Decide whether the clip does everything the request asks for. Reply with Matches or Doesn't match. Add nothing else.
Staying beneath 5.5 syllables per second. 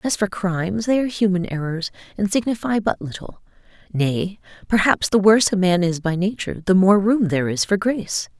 Doesn't match